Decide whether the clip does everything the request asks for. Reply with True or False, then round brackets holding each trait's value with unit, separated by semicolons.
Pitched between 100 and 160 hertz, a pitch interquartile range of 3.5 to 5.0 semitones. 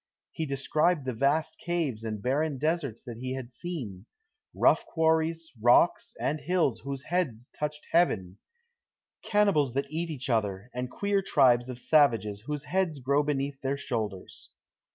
True (140 Hz; 4.7 semitones)